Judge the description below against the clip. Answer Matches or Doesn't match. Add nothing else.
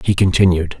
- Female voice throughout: Doesn't match